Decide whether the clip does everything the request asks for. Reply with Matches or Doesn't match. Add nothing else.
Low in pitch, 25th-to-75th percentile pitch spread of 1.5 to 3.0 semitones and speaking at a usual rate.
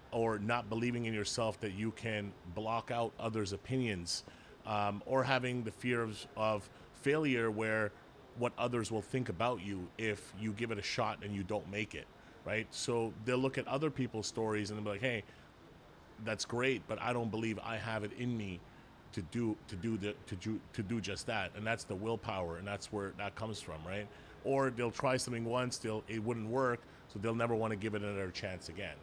Doesn't match